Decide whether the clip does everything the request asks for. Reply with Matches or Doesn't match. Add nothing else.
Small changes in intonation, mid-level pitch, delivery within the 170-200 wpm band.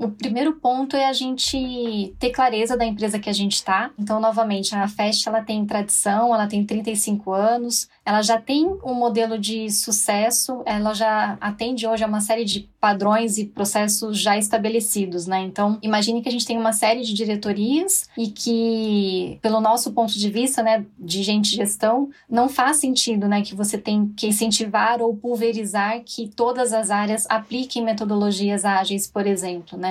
Doesn't match